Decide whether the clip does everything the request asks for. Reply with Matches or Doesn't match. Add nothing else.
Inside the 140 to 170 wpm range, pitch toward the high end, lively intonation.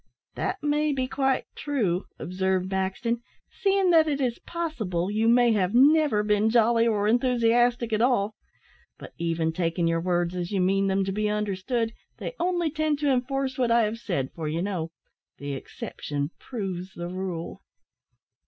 Matches